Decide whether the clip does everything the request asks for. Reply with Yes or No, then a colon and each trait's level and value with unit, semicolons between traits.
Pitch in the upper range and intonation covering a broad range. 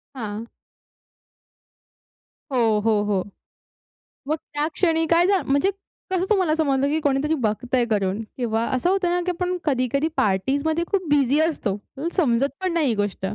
Yes: very high, 280 Hz; wide, 6.4 semitones